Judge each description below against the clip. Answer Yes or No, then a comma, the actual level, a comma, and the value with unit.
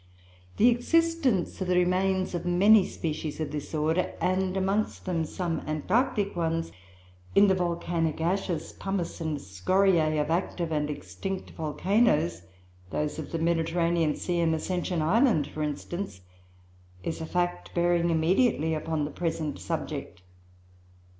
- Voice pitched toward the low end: No, medium, 170 Hz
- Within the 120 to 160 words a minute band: Yes, slow, 135 wpm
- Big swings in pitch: No, average, 3.2 semitones